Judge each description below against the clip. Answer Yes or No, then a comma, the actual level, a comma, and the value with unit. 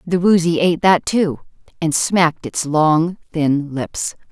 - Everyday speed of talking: Yes, average, 155 wpm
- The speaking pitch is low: No, medium, 165 Hz